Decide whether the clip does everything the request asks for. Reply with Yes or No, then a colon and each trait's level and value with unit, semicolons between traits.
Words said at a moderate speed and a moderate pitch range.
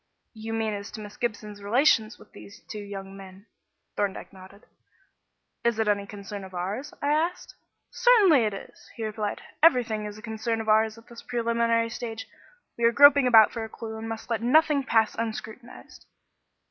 No: average, 180 wpm; narrow, 2.3 semitones